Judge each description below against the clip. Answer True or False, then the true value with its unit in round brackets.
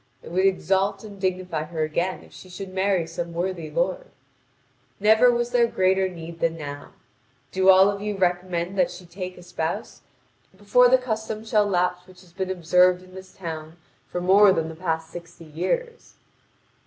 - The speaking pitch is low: False (185 Hz)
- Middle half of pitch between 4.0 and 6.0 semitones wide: False (2.6 semitones)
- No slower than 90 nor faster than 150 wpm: False (180 wpm)